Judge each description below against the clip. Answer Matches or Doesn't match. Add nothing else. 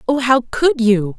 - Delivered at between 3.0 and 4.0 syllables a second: Matches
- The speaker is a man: Doesn't match